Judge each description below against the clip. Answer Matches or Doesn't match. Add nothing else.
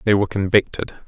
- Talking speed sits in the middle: Matches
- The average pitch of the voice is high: Doesn't match